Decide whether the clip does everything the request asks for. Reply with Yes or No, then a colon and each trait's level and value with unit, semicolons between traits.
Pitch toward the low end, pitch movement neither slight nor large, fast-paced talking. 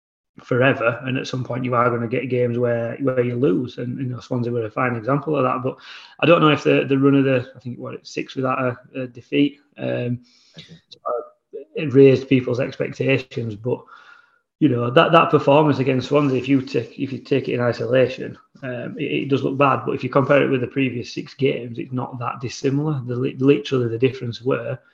No: low, 130 Hz; narrow, 2.3 semitones; fast, 220 wpm